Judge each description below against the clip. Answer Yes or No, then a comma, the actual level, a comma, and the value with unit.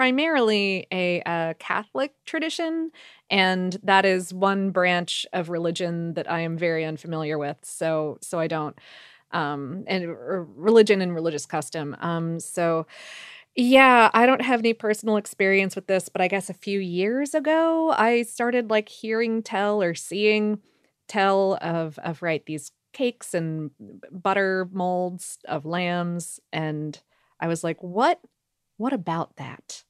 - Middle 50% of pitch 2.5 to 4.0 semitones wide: No, average, 4.5 semitones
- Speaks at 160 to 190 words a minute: No, average, 145 wpm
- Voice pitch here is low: No, medium, 185 Hz